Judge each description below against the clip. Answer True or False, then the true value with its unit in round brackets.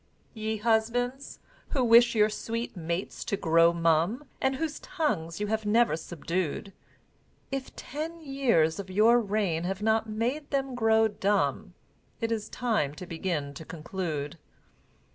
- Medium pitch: False (215 Hz)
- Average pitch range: False (6.0 semitones)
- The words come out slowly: False (145 wpm)